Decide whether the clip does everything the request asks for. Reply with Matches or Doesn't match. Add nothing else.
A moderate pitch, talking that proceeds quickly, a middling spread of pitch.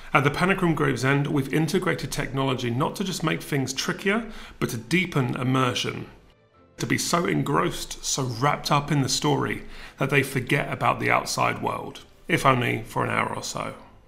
Doesn't match